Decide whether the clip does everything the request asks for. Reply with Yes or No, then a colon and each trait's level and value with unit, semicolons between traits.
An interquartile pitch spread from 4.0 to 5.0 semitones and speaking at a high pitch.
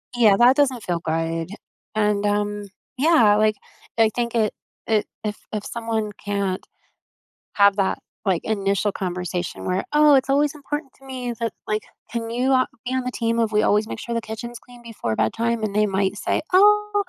No: average, 3.5 semitones; high, 220 Hz